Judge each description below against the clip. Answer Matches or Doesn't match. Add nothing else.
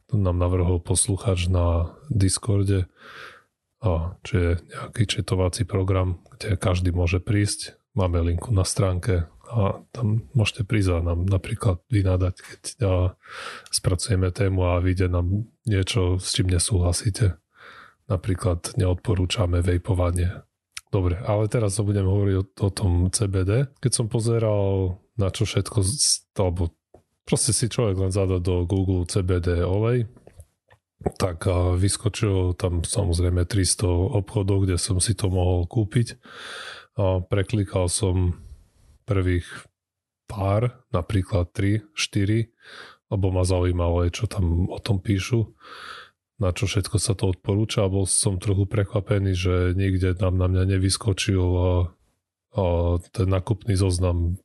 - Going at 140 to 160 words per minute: Doesn't match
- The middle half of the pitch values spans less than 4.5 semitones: Matches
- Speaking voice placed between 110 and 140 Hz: Doesn't match